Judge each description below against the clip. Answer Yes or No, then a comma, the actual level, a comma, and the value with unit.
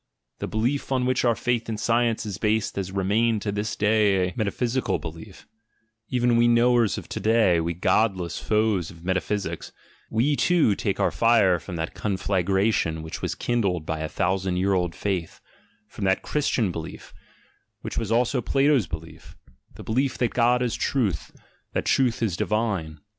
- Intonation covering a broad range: No, average, 4.2 semitones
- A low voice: Yes, low, 105 Hz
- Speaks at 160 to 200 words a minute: Yes, average, 170 wpm